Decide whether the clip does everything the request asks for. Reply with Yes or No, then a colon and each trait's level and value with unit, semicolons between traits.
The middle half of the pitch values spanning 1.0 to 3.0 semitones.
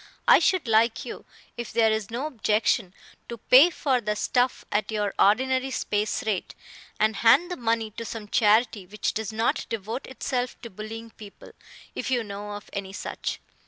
Yes: average, 2.7 semitones